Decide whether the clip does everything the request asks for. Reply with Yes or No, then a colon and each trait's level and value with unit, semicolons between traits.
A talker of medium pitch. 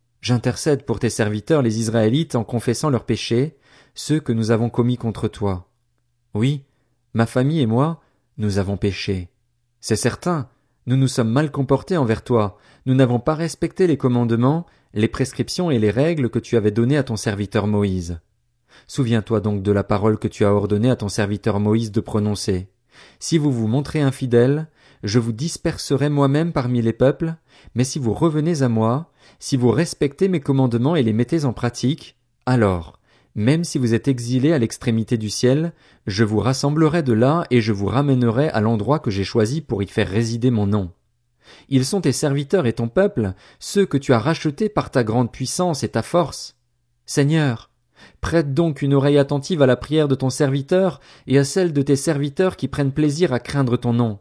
No: low, 125 Hz